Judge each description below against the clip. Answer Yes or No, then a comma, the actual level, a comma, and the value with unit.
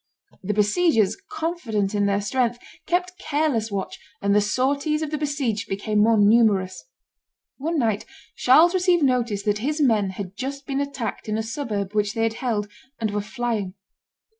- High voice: Yes, high, 225 Hz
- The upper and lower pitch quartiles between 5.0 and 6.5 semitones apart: Yes, wide, 5.5 semitones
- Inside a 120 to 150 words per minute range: No, average, 165 wpm